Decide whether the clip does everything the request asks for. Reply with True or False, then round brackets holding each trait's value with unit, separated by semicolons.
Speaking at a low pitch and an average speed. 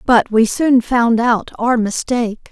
False (235 Hz; 165 wpm)